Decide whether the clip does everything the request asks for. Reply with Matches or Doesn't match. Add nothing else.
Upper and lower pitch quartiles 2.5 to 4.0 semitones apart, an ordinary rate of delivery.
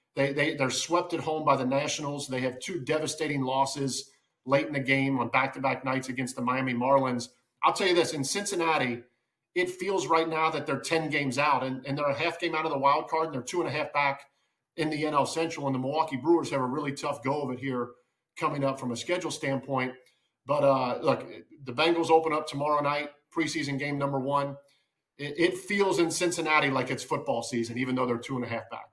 Doesn't match